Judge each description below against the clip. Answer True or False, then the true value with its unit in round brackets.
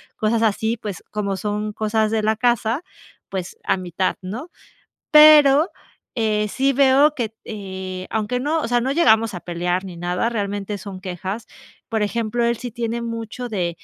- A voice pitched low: False (220 Hz)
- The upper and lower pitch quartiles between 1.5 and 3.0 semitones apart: False (3.4 semitones)